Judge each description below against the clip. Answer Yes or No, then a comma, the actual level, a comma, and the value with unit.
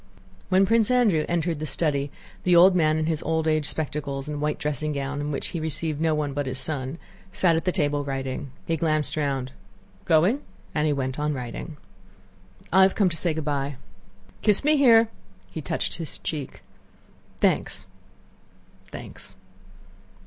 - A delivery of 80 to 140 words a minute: No, average, 170 wpm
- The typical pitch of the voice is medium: Yes, medium, 155 Hz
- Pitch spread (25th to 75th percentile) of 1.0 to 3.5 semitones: Yes, average, 2.9 semitones